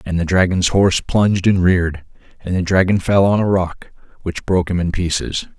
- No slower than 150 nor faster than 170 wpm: No, fast, 205 wpm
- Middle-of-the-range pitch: No, very low, 90 Hz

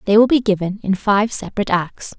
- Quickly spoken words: Yes, fast, 220 wpm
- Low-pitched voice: No, high, 205 Hz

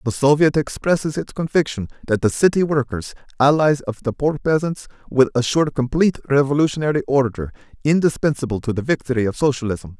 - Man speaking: Yes, male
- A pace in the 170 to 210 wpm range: No, average, 150 wpm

